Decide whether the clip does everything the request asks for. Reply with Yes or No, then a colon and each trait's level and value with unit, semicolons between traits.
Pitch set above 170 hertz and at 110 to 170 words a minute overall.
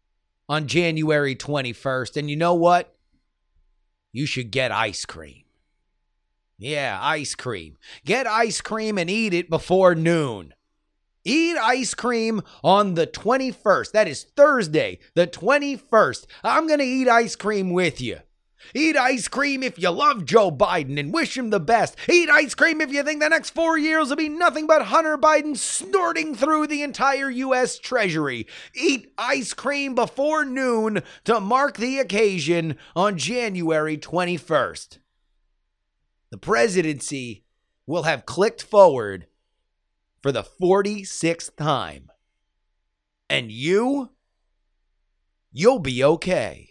Yes: medium, 185 Hz; slow, 135 wpm